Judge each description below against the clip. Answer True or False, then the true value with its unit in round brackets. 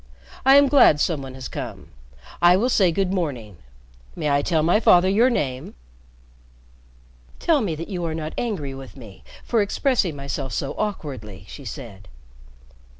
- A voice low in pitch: False (165 Hz)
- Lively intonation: True (7.0 semitones)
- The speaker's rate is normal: True (160 wpm)